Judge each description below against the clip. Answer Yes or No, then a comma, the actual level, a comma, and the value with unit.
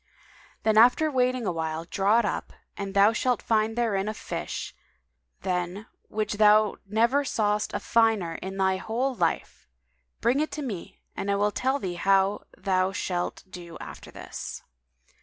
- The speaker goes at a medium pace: Yes, average, 160 wpm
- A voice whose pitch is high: Yes, high, 210 Hz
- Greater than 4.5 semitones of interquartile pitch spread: No, average, 3.4 semitones